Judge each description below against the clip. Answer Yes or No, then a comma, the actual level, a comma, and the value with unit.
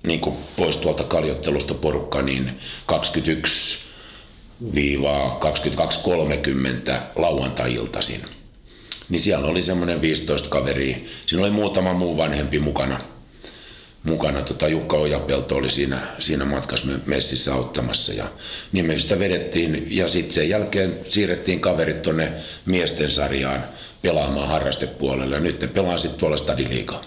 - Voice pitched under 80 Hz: Yes, very low, 70 Hz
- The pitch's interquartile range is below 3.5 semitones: No, average, 4.1 semitones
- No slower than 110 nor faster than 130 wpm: Yes, average, 120 wpm